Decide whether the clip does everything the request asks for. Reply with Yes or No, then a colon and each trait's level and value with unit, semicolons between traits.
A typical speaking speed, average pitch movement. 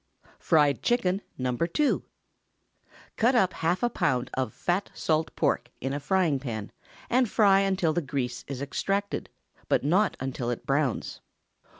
No: average, 150 wpm; wide, 6.6 semitones